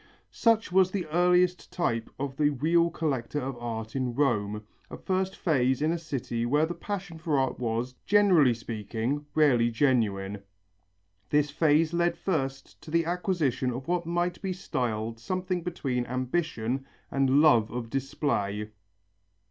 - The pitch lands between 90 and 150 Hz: Yes, medium, 140 Hz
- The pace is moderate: Yes, average, 150 wpm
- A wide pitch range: Yes, wide, 6.2 semitones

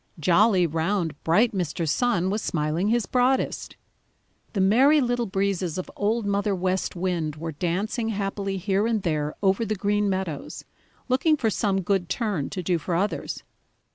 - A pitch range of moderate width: Yes, average, 3.8 semitones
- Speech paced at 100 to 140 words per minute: No, average, 160 wpm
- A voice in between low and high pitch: No, high, 195 Hz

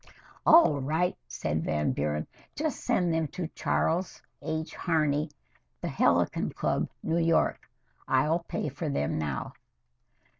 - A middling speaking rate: No, slow, 125 wpm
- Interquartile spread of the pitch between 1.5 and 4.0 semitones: No, average, 4.8 semitones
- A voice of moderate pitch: Yes, medium, 155 Hz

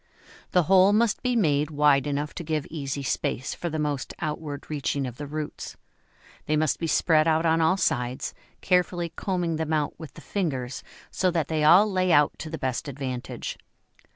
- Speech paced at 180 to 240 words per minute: Yes, average, 185 wpm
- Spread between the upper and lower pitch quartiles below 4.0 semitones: Yes, average, 3.3 semitones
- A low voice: No, medium, 155 Hz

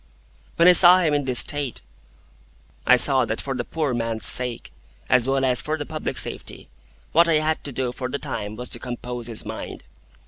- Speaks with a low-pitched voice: Yes, low, 130 Hz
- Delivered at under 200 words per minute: No, fast, 205 wpm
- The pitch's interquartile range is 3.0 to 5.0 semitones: Yes, average, 3.9 semitones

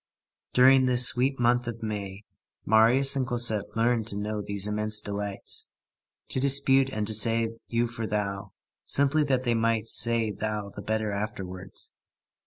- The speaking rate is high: No, average, 155 wpm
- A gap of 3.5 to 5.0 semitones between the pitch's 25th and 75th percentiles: No, average, 2.8 semitones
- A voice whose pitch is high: No, low, 110 Hz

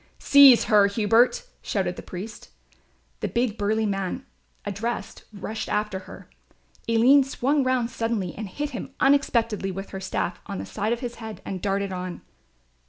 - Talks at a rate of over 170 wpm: No, average, 160 wpm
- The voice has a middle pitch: No, high, 220 Hz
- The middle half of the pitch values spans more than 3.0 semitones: Yes, average, 3.7 semitones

